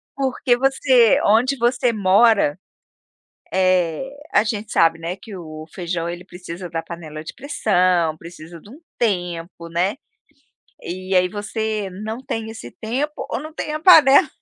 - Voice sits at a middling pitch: No, high, 195 Hz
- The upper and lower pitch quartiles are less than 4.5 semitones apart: No, wide, 5.6 semitones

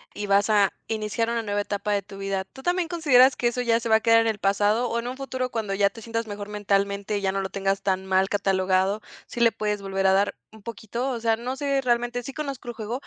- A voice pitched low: No, high, 215 Hz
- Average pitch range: Yes, average, 3.3 semitones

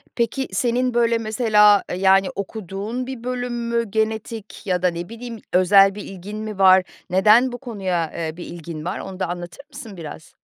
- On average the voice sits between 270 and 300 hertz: No, high, 210 Hz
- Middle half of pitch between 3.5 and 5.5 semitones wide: Yes, average, 4.0 semitones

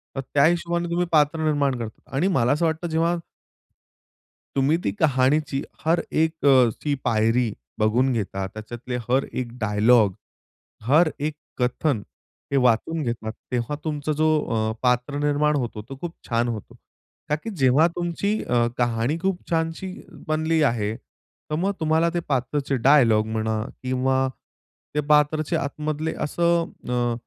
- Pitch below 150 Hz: Yes, medium, 140 Hz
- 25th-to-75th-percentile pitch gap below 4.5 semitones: No, average, 4.8 semitones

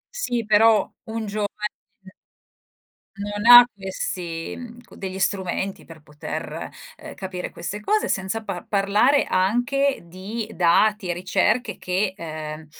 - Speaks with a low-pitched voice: No, high, 200 Hz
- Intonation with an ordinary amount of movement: Yes, average, 3.5 semitones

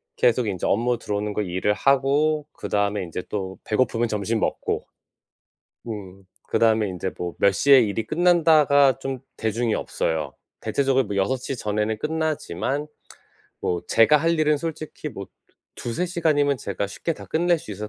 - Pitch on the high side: No, low, 115 Hz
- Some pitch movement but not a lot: No, wide, 6.2 semitones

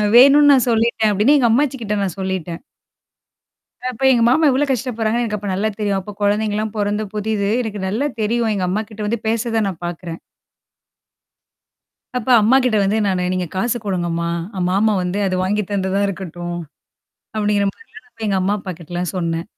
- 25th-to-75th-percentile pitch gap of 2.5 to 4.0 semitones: Yes, average, 3.4 semitones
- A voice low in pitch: No, high, 210 Hz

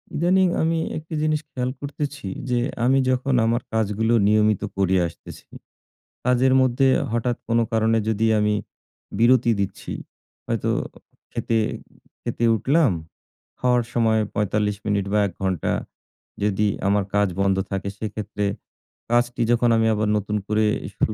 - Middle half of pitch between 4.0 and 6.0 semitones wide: No, average, 3.2 semitones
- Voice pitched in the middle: No, low, 115 Hz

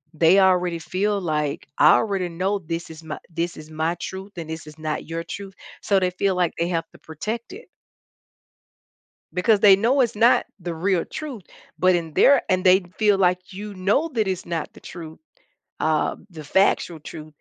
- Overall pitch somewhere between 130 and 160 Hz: No, medium, 180 Hz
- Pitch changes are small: No, average, 3.5 semitones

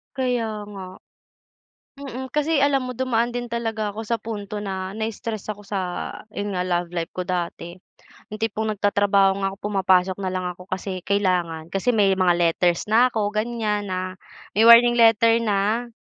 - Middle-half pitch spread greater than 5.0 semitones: No, average, 3.5 semitones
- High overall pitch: Yes, high, 205 Hz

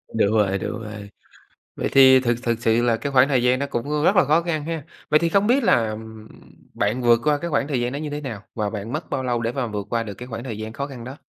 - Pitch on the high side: No, low, 125 Hz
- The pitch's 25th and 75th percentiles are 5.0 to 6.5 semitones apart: No, average, 4.5 semitones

